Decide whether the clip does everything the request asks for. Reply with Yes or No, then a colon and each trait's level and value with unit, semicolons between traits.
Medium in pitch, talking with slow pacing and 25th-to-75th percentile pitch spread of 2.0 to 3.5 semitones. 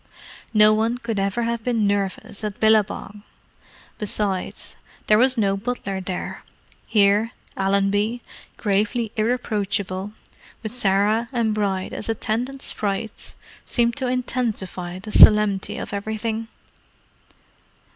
No: high, 215 Hz; slow, 110 wpm; narrow, 2.6 semitones